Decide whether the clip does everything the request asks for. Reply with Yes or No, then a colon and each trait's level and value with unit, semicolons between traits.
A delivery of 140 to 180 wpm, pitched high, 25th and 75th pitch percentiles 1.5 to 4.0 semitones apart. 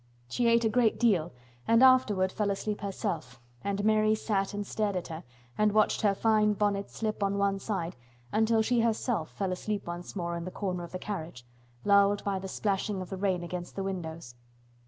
No: average, 200 wpm; high, 200 Hz; average, 2.8 semitones